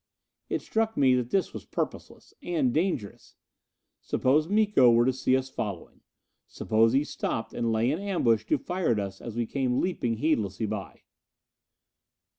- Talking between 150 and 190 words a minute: Yes, average, 160 wpm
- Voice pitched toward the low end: Yes, low, 130 Hz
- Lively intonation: Yes, wide, 6.8 semitones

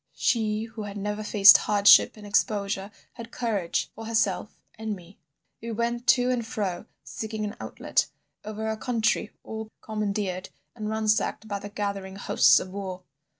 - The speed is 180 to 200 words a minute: No, average, 155 wpm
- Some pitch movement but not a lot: No, narrow, 1.7 semitones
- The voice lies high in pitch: Yes, high, 210 Hz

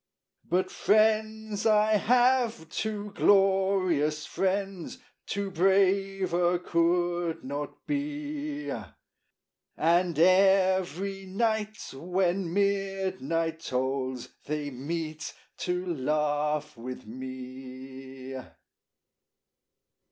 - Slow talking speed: Yes, slow, 70 wpm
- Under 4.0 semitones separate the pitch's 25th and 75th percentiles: No, average, 4.7 semitones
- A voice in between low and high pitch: Yes, medium, 180 Hz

